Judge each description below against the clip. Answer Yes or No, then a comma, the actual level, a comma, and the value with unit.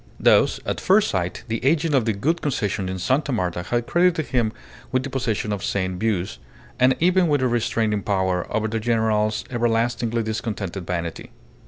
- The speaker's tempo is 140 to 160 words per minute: No, average, 175 wpm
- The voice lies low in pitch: Yes, low, 115 Hz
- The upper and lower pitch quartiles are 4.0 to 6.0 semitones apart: Yes, average, 4.5 semitones